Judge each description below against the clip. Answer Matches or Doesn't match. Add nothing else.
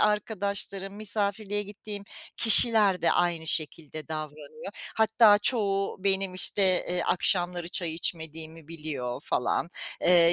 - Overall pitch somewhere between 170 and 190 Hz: Matches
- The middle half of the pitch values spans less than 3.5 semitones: Doesn't match